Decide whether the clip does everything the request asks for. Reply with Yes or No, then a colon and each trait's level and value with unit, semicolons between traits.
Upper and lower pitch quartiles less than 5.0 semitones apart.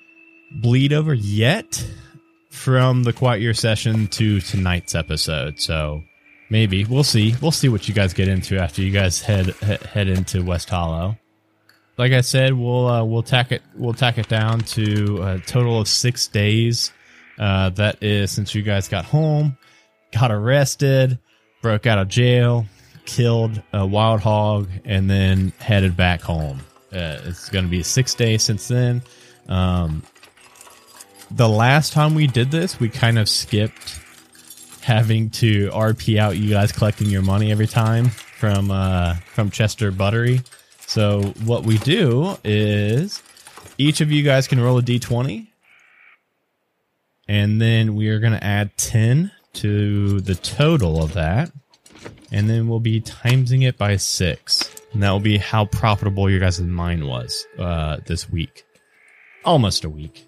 Yes: average, 3.9 semitones